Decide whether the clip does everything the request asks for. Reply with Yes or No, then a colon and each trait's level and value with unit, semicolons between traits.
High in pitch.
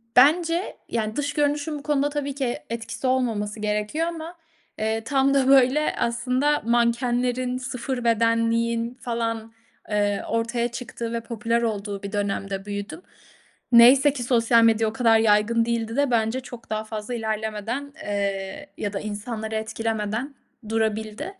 Yes: high, 230 Hz